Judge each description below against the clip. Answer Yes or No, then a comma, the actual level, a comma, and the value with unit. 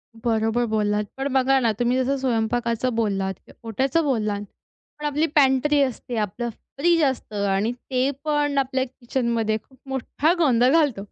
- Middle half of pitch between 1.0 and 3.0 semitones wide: No, average, 3.5 semitones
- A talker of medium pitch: No, very high, 250 Hz